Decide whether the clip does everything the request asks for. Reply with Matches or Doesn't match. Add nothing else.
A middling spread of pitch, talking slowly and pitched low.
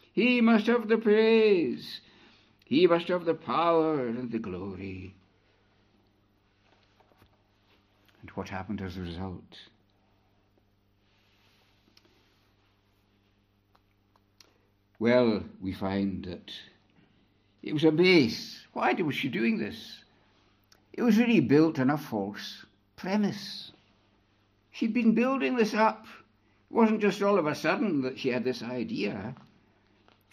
Doesn't match